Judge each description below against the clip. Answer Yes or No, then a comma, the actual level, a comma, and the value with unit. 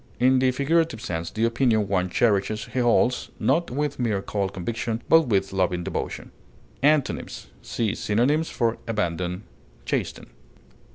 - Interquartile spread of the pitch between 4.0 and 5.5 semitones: Yes, average, 4.8 semitones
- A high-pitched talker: No, low, 115 Hz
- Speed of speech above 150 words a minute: No, slow, 135 wpm